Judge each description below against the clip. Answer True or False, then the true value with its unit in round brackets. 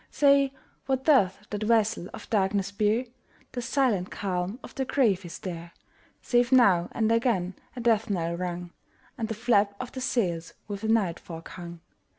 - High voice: True (210 Hz)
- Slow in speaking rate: False (165 wpm)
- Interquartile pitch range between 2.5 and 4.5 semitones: False (4.9 semitones)